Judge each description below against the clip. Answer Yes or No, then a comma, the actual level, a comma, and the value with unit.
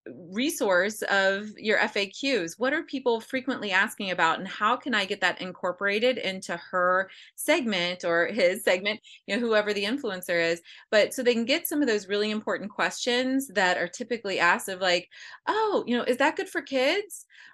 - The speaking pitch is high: Yes, high, 210 Hz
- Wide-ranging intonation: Yes, wide, 5.7 semitones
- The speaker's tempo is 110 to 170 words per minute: No, average, 185 wpm